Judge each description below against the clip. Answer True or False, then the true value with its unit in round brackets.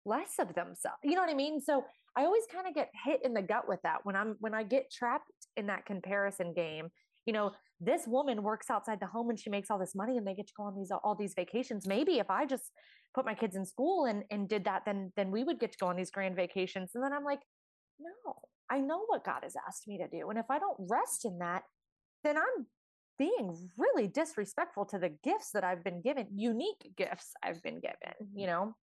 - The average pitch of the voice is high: True (220 Hz)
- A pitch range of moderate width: False (5.7 semitones)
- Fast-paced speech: True (245 wpm)